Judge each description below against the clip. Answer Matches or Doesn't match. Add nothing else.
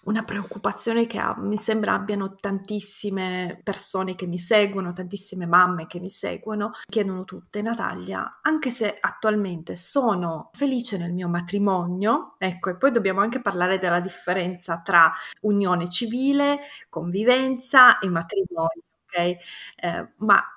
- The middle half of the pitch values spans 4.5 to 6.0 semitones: Doesn't match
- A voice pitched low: Doesn't match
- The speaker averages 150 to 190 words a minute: Doesn't match